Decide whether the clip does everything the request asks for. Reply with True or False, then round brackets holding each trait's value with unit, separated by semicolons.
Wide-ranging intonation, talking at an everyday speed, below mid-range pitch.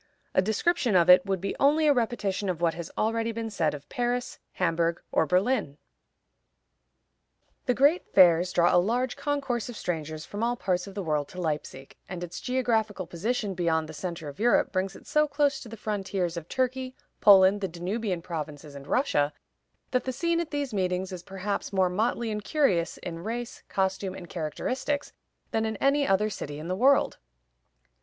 False (5.9 semitones; 185 wpm; 195 Hz)